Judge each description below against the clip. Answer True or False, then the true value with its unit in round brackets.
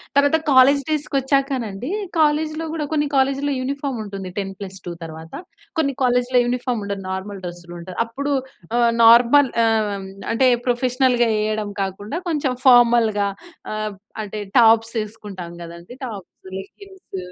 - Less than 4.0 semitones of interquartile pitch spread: False (5.4 semitones)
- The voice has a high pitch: True (235 Hz)